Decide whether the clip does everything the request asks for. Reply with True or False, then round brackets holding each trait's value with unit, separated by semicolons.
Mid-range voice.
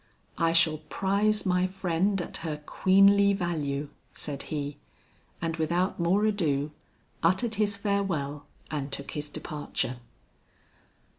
True (170 Hz)